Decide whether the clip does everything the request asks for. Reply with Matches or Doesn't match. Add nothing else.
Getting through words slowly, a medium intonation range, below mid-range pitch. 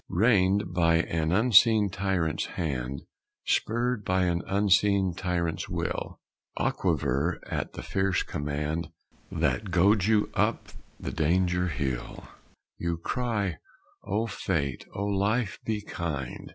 Matches